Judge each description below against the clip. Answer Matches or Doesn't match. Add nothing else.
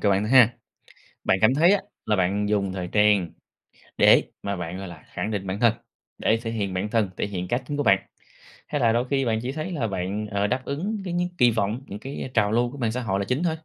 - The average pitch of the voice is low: Matches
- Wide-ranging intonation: Doesn't match